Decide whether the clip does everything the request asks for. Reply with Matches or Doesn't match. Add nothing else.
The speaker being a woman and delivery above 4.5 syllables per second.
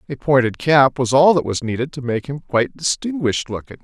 Doesn't match